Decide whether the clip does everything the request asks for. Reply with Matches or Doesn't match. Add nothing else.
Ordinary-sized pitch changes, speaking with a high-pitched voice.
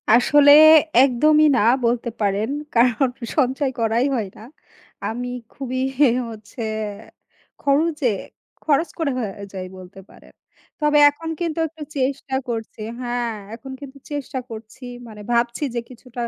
Matches